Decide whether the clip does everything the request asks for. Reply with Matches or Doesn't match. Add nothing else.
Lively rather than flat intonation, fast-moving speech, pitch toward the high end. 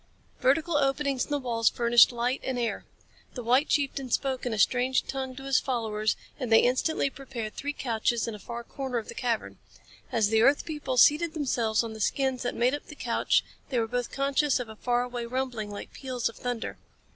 Doesn't match